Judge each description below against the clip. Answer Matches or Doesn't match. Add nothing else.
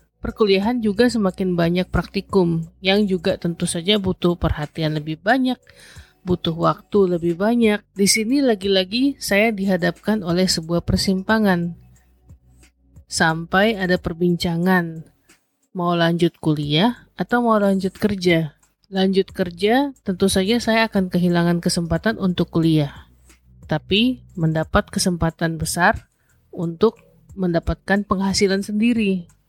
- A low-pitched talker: Doesn't match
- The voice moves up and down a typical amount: Matches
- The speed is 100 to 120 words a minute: Matches